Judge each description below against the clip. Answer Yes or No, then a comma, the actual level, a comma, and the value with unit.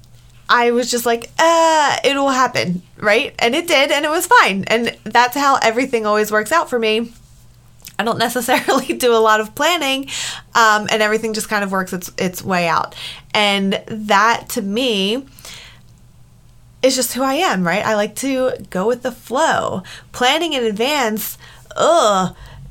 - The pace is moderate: Yes, average, 170 wpm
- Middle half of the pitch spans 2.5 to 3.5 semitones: No, average, 4.5 semitones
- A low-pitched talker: No, high, 230 Hz